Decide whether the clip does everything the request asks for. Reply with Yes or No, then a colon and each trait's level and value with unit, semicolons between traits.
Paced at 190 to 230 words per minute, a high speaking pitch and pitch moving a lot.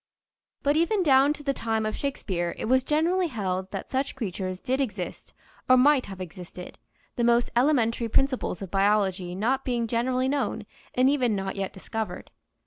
No: average, 170 wpm; high, 235 Hz; wide, 5.7 semitones